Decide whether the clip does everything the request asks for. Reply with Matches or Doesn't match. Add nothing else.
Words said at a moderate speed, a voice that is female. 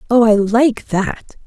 Matches